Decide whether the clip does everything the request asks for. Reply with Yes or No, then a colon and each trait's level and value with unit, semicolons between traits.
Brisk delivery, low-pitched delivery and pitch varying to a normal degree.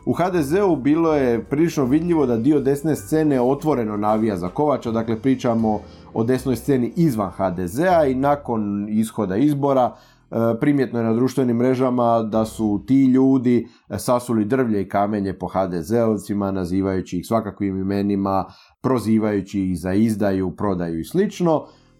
No: average, 140 wpm; low, 115 Hz; average, 4.8 semitones